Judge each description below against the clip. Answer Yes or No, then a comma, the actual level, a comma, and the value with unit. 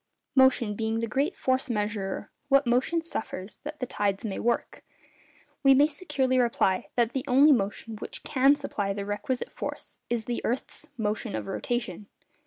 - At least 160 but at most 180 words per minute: Yes, average, 165 wpm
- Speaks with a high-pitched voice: Yes, high, 240 Hz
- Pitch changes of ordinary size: Yes, average, 4.5 semitones